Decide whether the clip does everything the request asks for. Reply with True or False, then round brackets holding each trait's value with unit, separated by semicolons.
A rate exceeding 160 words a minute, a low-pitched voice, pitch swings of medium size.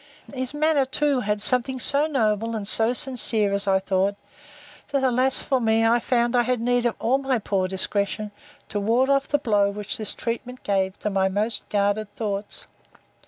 False (185 wpm; 225 Hz; 4.0 semitones)